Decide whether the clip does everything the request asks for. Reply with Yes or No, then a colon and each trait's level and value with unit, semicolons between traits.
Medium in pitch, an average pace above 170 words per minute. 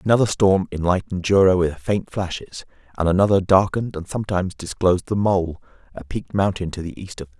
No: very low, 95 Hz; average, 195 wpm